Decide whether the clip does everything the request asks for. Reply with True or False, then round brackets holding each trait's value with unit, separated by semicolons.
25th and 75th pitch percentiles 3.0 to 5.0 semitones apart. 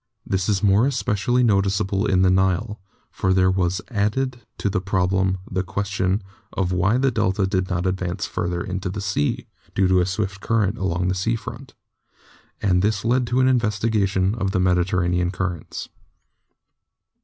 False (2.4 semitones)